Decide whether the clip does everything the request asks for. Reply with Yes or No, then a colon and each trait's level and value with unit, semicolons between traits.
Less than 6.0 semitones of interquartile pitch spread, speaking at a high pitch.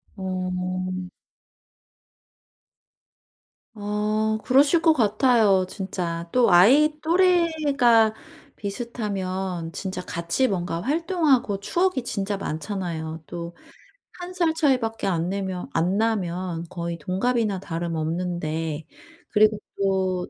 Yes: average, 5.3 semitones; high, 195 Hz